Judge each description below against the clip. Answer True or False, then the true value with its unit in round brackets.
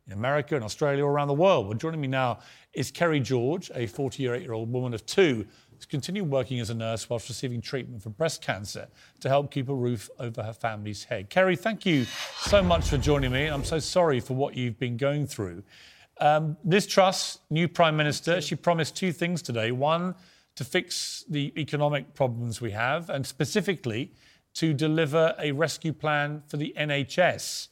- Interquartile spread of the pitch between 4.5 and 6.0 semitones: True (4.8 semitones)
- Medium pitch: True (145 Hz)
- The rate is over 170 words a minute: True (190 wpm)